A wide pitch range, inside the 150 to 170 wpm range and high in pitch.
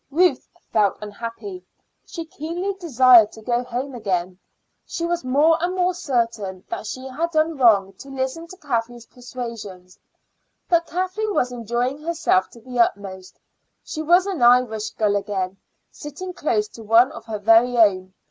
Yes: wide, 7.0 semitones; average, 155 wpm; high, 245 Hz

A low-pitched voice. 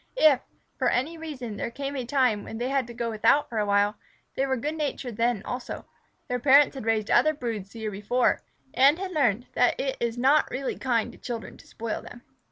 No: high, 245 Hz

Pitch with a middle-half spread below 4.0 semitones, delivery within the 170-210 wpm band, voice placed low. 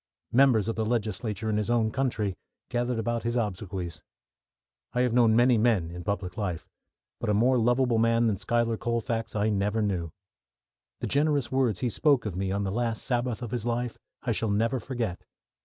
Yes: average, 2.8 semitones; average, 190 wpm; low, 115 Hz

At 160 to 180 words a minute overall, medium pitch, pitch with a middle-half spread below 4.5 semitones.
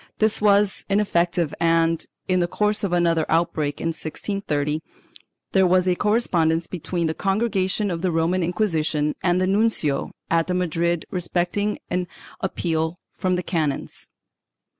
No: average, 140 wpm; medium, 175 Hz; average, 2.7 semitones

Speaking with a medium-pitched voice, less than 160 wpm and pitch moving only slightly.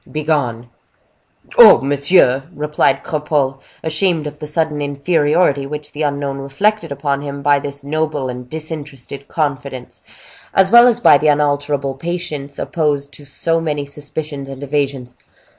Yes: medium, 145 Hz; average, 140 wpm; narrow, 1.8 semitones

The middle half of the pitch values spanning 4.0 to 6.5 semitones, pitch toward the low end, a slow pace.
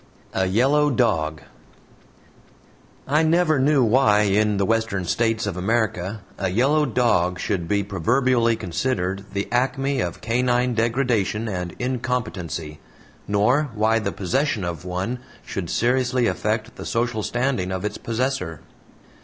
Yes: average, 4.7 semitones; low, 115 Hz; slow, 130 wpm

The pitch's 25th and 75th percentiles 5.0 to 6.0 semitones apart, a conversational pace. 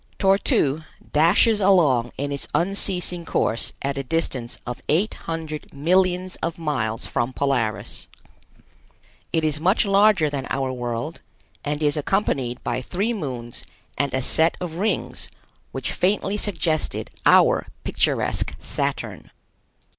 No: wide, 5.6 semitones; slow, 130 wpm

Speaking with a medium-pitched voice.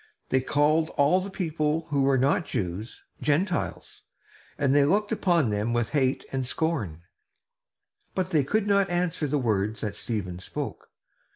Yes: medium, 145 Hz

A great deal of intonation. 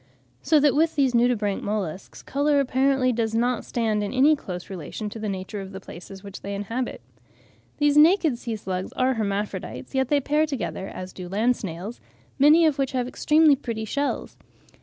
Yes: wide, 5.8 semitones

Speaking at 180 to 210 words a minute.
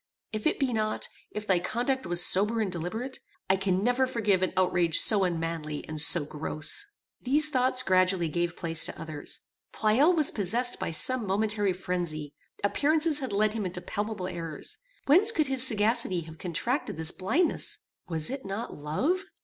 No: average, 170 wpm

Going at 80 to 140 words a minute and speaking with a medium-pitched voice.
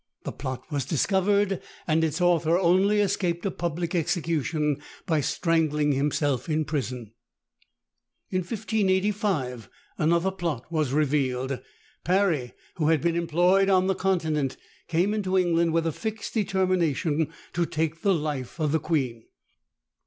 Yes: slow, 135 wpm; medium, 165 Hz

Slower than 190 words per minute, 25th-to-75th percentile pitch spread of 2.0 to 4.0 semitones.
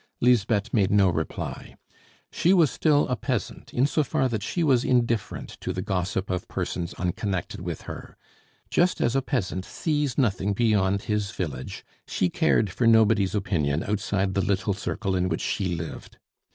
No: average, 165 wpm; average, 4.5 semitones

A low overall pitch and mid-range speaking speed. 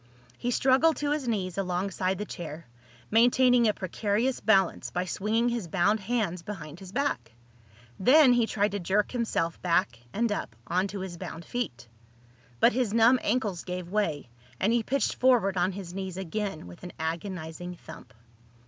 No: high, 195 Hz; average, 165 wpm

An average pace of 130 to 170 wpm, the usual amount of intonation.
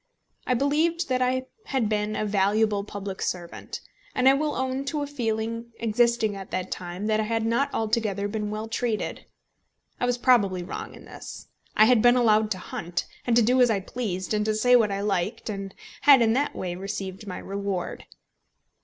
No: average, 195 wpm; average, 3.7 semitones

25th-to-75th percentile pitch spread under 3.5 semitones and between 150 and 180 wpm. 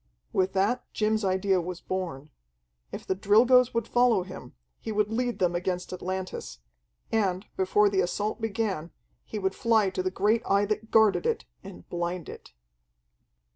Yes: average, 3.1 semitones; average, 160 wpm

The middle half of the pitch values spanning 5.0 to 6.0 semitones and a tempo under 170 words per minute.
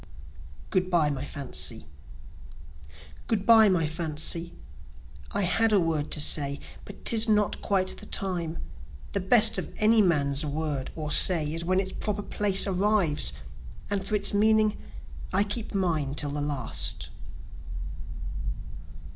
Yes: wide, 5.4 semitones; average, 140 wpm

